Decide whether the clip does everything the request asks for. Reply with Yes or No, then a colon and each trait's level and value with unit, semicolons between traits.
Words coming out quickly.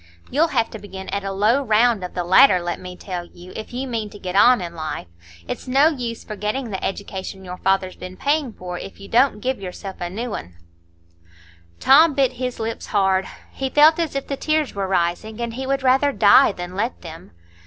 Yes: fast, 215 wpm